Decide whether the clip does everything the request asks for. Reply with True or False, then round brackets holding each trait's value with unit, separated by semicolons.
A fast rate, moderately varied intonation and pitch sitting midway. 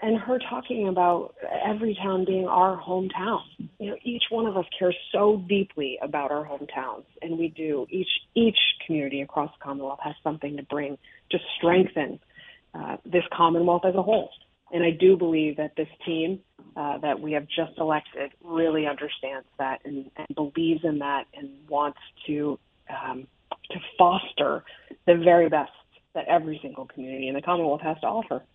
False (170 wpm; 4.2 semitones; 160 Hz)